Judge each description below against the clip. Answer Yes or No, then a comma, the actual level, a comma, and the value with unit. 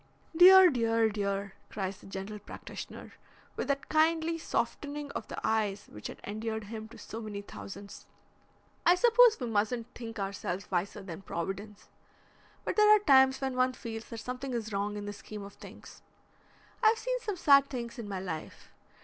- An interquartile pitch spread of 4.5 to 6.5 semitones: Yes, wide, 5.6 semitones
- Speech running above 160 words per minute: Yes, average, 175 wpm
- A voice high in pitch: Yes, high, 225 Hz